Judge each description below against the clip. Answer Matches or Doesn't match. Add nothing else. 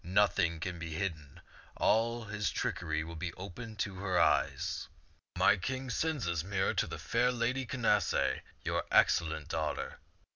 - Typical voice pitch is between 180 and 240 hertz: Doesn't match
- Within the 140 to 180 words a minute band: Matches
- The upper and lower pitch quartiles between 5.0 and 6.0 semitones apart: Matches